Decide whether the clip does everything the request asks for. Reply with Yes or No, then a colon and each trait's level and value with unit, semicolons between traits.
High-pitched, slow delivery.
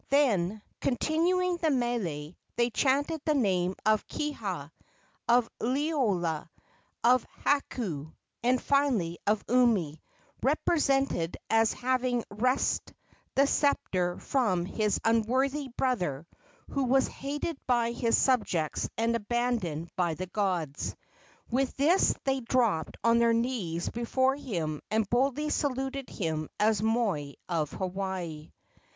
Yes: high, 235 Hz; slow, 115 wpm